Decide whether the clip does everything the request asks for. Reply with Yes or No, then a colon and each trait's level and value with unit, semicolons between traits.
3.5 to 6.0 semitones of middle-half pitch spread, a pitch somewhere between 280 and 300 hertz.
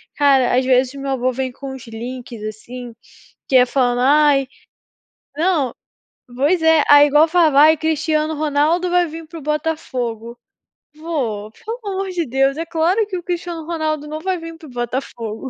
Yes: average, 4.2 semitones; very high, 290 Hz